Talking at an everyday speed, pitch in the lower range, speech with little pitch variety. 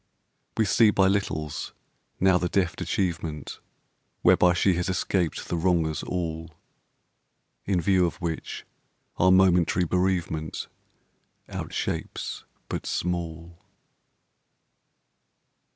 No: slow, 95 wpm; very low, 90 Hz; narrow, 2.1 semitones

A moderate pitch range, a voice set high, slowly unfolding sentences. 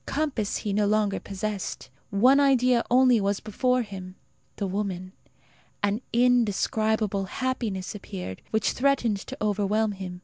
Yes: average, 3.7 semitones; high, 210 Hz; slow, 130 wpm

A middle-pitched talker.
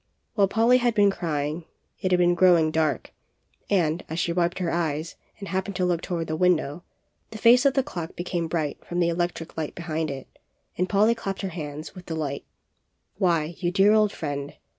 Yes: medium, 175 Hz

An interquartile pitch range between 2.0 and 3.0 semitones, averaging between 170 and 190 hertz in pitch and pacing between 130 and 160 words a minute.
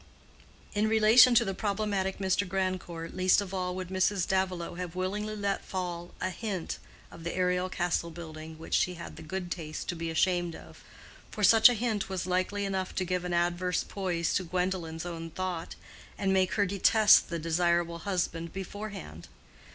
No: narrow, 2.4 semitones; medium, 185 Hz; average, 175 wpm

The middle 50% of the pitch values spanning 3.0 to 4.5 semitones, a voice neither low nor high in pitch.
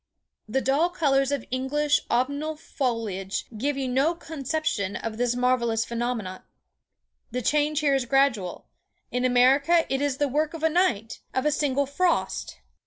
No: average, 3.4 semitones; very high, 270 Hz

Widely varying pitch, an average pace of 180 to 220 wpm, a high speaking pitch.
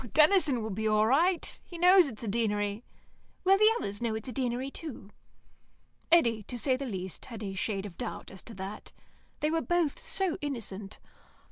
Yes: wide, 6.7 semitones; average, 195 wpm; high, 235 Hz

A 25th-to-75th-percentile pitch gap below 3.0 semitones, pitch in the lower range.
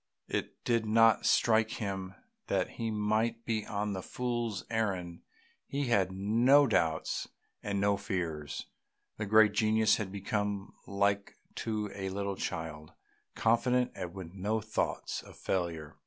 Yes: narrow, 2.6 semitones; low, 105 Hz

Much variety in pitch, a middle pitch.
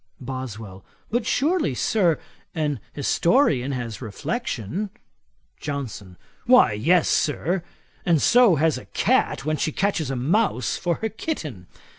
Yes: wide, 8.2 semitones; medium, 155 Hz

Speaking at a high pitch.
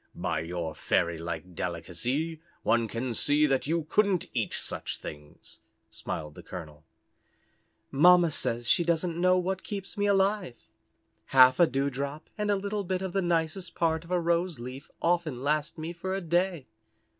No: medium, 160 Hz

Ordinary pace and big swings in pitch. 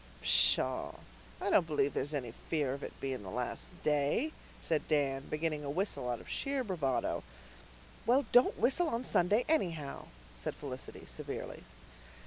Yes: average, 150 wpm; wide, 7.4 semitones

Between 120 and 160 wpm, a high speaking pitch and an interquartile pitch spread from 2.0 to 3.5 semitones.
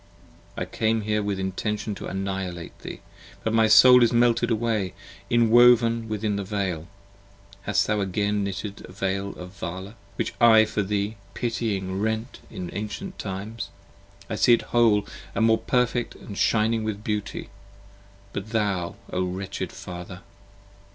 No: average, 150 wpm; low, 105 Hz; average, 2.7 semitones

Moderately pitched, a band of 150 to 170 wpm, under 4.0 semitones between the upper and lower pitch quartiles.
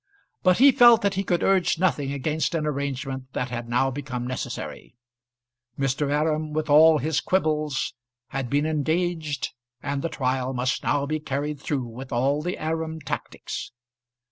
Yes: medium, 145 Hz; average, 160 wpm; average, 3.1 semitones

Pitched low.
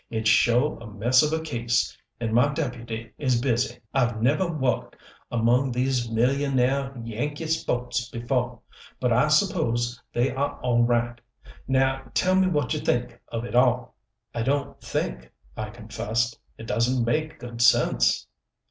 Yes: low, 120 Hz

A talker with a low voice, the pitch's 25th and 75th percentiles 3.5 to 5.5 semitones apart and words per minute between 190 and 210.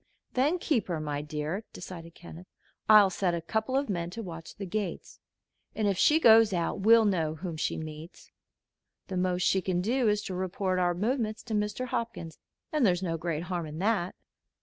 No: medium, 185 Hz; average, 4.3 semitones; average, 195 wpm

